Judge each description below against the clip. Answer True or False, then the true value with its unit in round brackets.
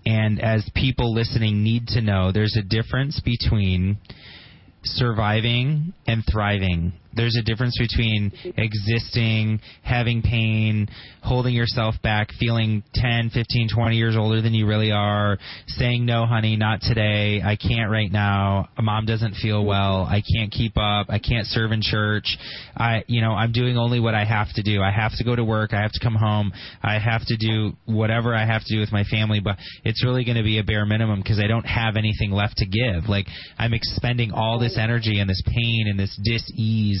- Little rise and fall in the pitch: True (1.8 semitones)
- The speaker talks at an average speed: True (195 wpm)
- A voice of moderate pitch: False (110 Hz)